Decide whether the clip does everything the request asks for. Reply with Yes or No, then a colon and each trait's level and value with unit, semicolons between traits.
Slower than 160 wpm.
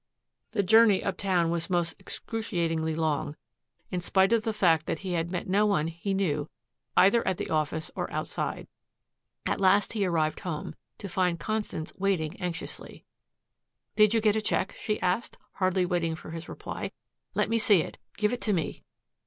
No: average, 175 wpm